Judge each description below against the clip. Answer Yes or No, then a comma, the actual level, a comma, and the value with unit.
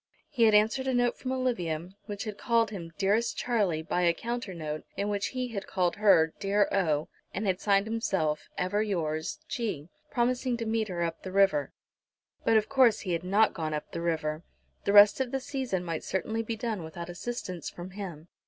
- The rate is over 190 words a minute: Yes, average, 200 wpm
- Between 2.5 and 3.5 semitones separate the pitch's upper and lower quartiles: No, average, 5.1 semitones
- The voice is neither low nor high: No, high, 200 Hz